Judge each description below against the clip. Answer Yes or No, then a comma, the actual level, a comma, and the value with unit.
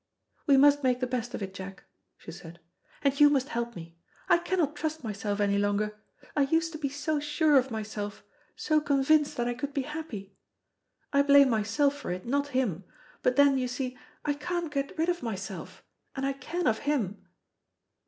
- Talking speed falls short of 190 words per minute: No, average, 195 wpm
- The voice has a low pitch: No, very high, 270 Hz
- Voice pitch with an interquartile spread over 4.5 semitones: Yes, average, 5.3 semitones